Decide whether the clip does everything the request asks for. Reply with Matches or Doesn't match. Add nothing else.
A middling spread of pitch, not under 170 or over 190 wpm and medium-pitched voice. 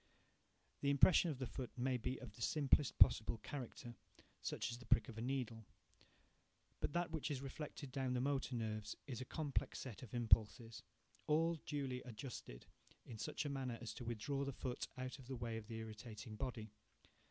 Doesn't match